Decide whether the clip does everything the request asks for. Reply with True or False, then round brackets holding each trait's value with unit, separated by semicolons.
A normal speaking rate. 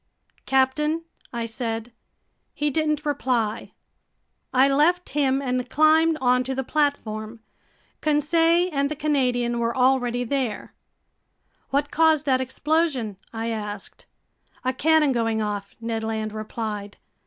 False (120 wpm)